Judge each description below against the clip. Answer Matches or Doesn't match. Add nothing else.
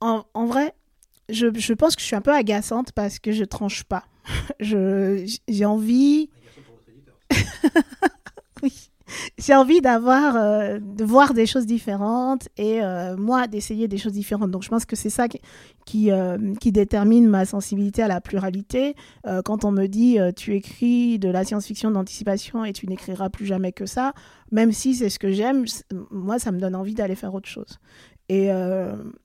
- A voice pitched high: Matches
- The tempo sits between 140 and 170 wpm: Doesn't match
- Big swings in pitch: Doesn't match